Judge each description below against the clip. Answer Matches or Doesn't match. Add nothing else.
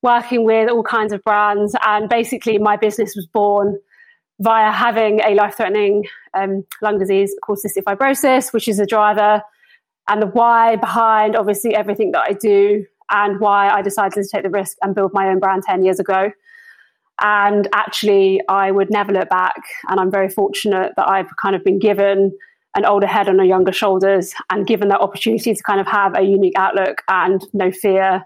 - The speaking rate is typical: Matches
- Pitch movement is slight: Matches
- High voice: Matches